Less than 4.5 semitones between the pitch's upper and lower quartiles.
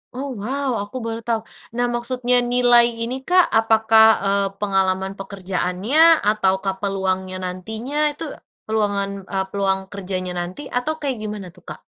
Yes: average, 4.0 semitones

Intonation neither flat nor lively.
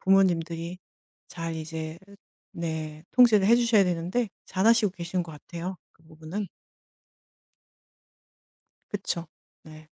Yes: average, 3.2 semitones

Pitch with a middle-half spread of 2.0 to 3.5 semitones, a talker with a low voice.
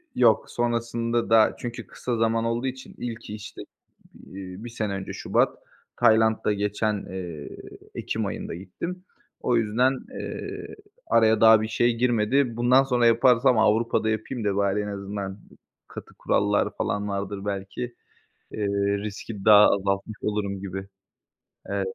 Yes: average, 2.8 semitones; low, 110 Hz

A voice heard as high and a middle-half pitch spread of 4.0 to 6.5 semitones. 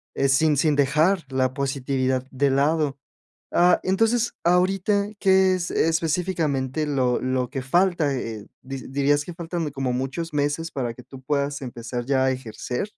No: medium, 140 Hz; average, 4.3 semitones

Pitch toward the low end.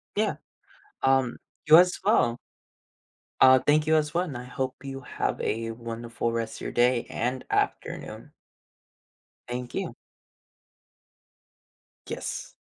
Yes: low, 125 Hz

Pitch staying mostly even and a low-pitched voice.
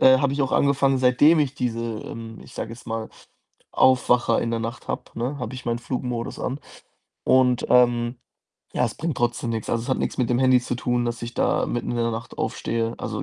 Yes: narrow, 1.9 semitones; low, 120 Hz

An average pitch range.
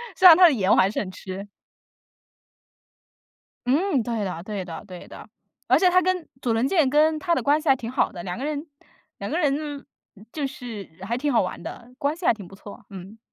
No: wide, 7.4 semitones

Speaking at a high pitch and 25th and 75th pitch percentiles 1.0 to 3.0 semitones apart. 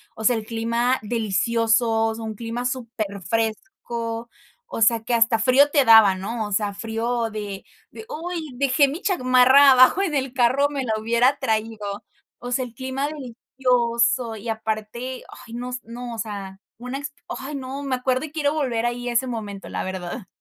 Yes: high, 235 Hz; average, 2.7 semitones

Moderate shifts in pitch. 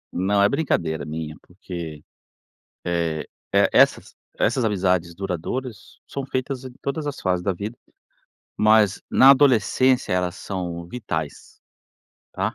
No: wide, 6.7 semitones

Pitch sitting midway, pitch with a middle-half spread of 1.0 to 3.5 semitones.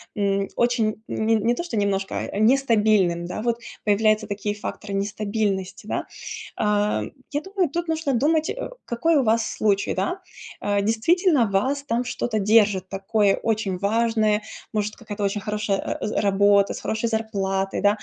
No: high, 215 Hz; average, 2.8 semitones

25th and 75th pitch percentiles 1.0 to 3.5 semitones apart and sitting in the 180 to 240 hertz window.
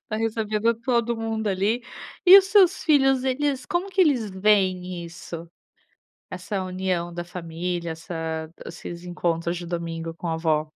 No: wide, 5.4 semitones; medium, 185 Hz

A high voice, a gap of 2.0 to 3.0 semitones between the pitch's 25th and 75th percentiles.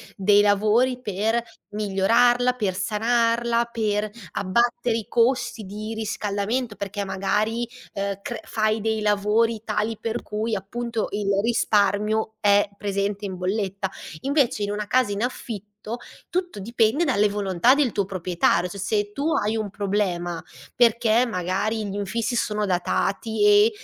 Yes: high, 210 Hz; narrow, 2.5 semitones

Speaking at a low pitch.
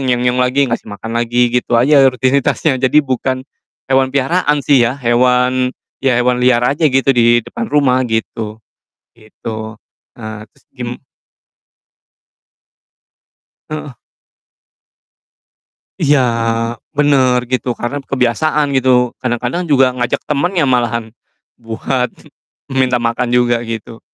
Yes: low, 125 Hz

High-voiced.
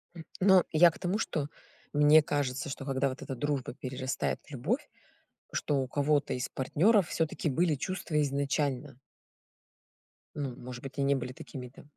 No: medium, 145 Hz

